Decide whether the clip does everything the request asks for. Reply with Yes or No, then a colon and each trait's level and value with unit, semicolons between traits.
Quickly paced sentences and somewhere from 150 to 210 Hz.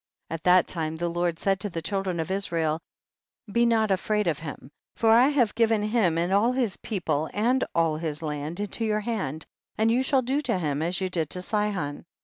Yes: fast, 215 wpm; high, 190 Hz